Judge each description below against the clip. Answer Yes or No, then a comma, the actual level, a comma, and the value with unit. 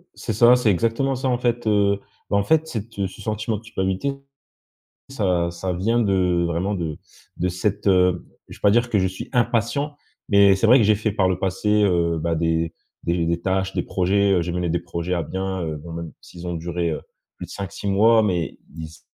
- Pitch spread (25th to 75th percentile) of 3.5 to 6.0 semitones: Yes, average, 4.0 semitones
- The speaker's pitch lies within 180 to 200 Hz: No, very low, 95 Hz